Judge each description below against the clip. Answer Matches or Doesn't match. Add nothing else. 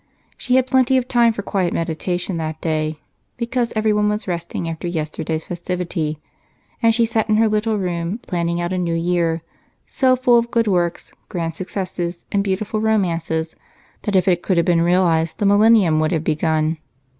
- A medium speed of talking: Matches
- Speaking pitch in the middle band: Matches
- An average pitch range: Matches